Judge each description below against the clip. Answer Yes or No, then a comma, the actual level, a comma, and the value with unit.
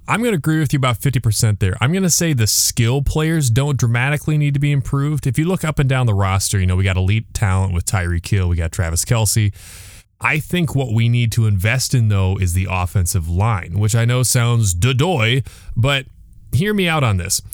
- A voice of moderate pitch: No, low, 115 Hz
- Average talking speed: No, fast, 235 wpm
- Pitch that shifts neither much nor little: No, wide, 6.3 semitones